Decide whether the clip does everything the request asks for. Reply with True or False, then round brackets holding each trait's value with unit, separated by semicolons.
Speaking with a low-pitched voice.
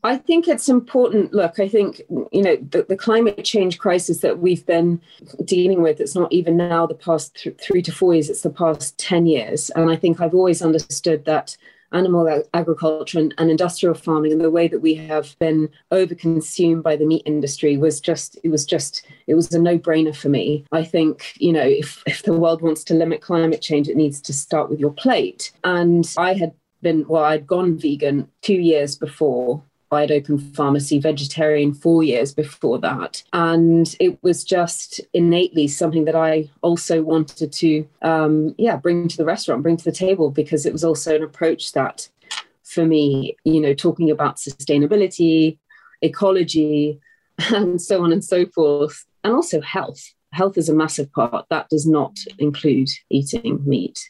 False (160 Hz)